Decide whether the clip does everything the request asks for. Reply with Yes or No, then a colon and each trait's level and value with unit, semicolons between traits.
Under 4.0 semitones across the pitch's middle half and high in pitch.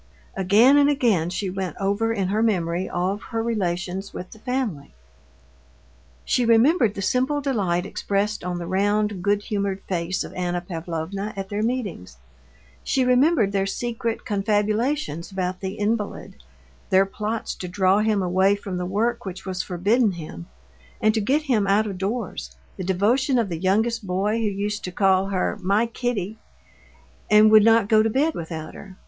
Yes: average, 3.4 semitones; high, 200 Hz